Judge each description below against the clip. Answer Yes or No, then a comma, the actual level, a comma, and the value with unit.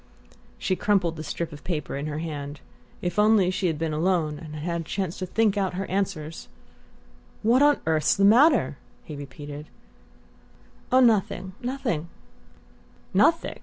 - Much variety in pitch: No, average, 5.0 semitones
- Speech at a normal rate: Yes, average, 155 wpm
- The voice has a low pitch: No, medium, 175 Hz